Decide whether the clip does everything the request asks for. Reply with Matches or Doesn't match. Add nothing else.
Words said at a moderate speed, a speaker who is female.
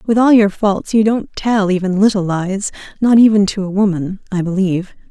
Matches